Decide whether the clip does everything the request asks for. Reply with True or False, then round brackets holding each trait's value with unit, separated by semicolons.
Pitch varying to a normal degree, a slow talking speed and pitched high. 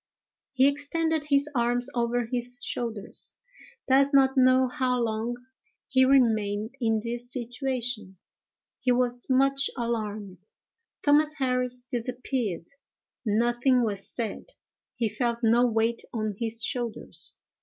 False (2.3 semitones; 115 wpm; 245 Hz)